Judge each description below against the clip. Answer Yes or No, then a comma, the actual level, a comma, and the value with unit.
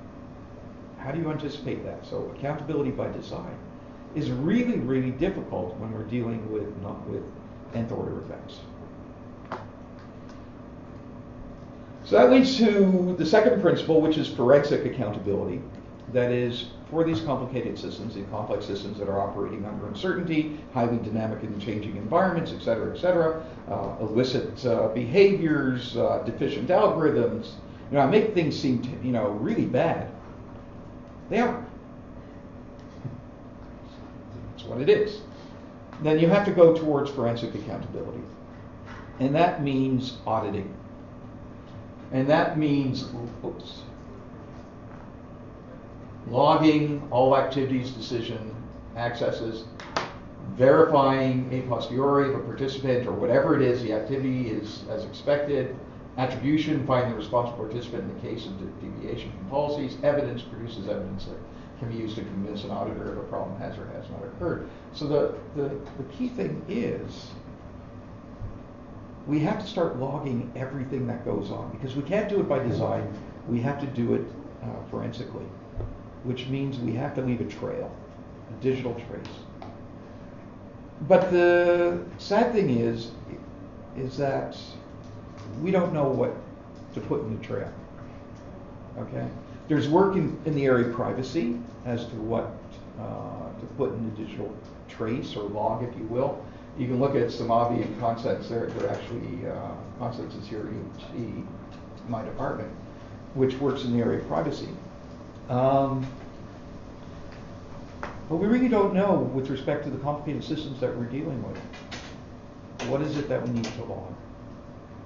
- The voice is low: Yes, low, 120 Hz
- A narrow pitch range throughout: No, average, 3.8 semitones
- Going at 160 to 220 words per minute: No, average, 145 wpm